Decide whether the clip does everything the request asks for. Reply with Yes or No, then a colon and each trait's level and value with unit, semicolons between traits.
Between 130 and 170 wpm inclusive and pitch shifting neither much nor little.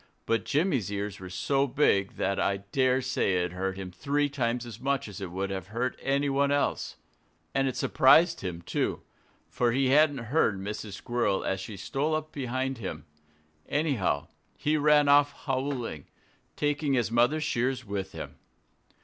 No: average, 165 wpm; wide, 6.3 semitones